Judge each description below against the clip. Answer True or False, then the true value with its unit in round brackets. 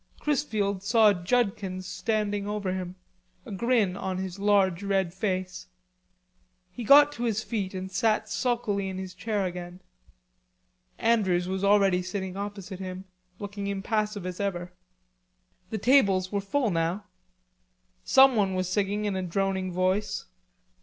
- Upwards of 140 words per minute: False (135 wpm)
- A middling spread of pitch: False (2.3 semitones)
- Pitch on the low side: False (195 Hz)